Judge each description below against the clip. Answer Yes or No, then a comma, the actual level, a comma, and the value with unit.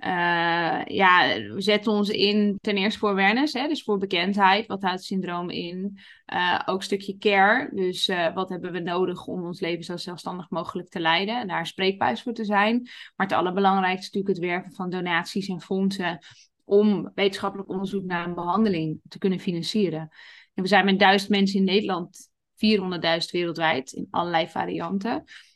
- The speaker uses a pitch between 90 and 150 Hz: No, high, 190 Hz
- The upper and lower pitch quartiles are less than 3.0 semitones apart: Yes, narrow, 2.4 semitones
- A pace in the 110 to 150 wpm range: No, average, 180 wpm